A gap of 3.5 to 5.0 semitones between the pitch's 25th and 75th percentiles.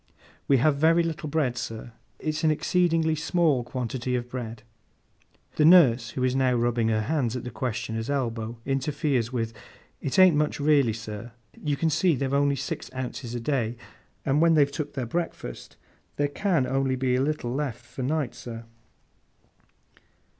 Yes: average, 4.0 semitones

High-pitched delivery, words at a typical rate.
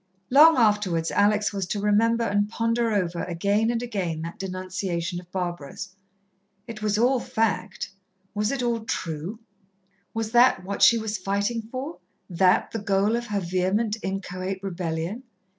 Yes: high, 205 Hz; average, 150 wpm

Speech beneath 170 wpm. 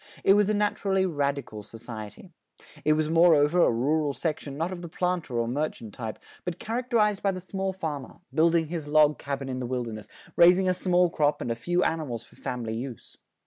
No: average, 190 wpm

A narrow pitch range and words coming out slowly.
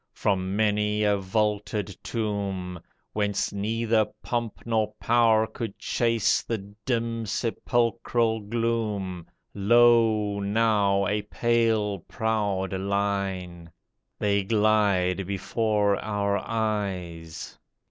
Yes: narrow, 2.3 semitones; slow, 90 wpm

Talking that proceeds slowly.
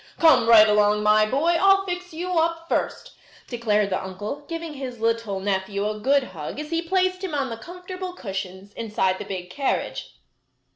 No: average, 180 wpm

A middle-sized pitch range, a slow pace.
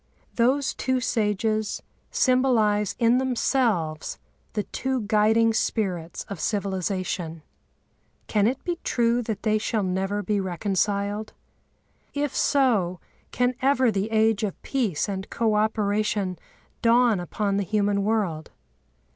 Yes: average, 3.0 semitones; slow, 120 wpm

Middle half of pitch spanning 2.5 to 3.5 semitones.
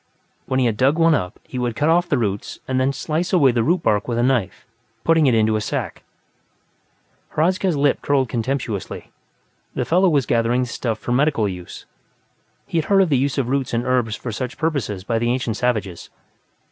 No: average, 4.5 semitones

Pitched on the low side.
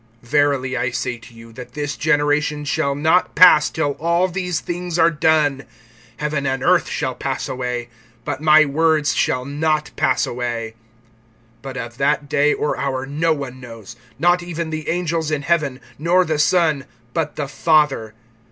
No: medium, 150 Hz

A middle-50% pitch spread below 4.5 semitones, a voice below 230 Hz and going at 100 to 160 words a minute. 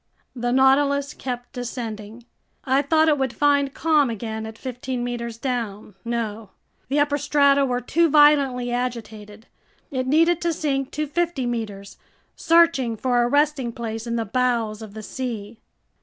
No: average, 3.7 semitones; very high, 250 Hz; average, 155 wpm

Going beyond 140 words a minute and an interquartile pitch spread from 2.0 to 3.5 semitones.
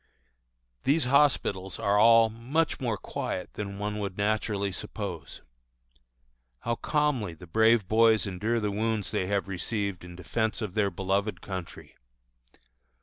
No: slow, 135 wpm; average, 2.9 semitones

